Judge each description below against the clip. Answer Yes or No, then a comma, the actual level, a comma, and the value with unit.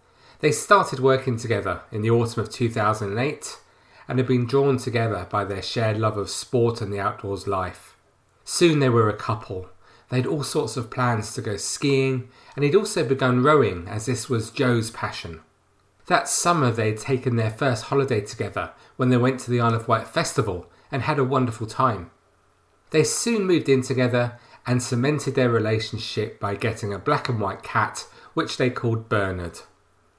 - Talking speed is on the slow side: No, average, 175 wpm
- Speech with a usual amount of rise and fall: Yes, average, 4.2 semitones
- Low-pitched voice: Yes, low, 120 Hz